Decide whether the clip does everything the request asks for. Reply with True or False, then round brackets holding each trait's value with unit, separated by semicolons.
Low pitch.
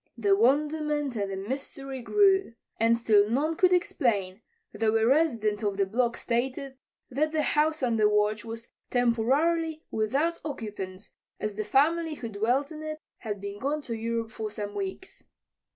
False (235 Hz)